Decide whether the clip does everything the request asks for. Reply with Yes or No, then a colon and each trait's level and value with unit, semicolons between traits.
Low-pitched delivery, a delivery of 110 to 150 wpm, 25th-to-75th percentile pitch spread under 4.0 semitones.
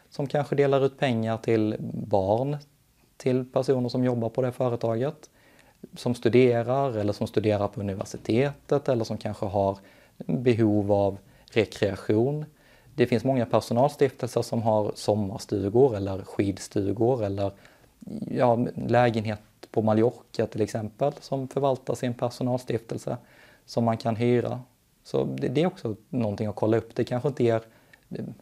Yes: low, 120 Hz; average, 135 wpm; average, 3.3 semitones